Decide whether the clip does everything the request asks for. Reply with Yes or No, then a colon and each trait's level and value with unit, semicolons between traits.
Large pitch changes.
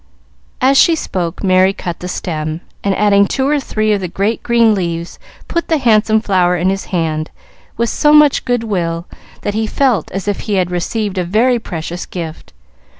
No: average, 4.6 semitones